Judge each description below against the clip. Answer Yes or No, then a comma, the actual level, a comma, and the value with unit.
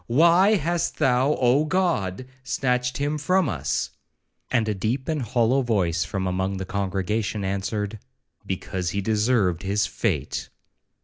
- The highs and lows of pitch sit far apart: Yes, wide, 6.1 semitones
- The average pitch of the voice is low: Yes, low, 110 Hz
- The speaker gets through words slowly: Yes, slow, 125 wpm